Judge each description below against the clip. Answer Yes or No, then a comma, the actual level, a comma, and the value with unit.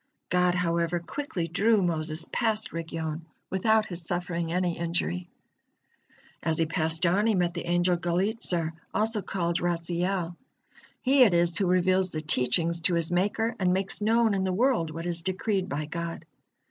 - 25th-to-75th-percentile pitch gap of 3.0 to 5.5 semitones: No, narrow, 2.4 semitones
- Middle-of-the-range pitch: Yes, medium, 175 Hz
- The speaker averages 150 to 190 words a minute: Yes, average, 160 wpm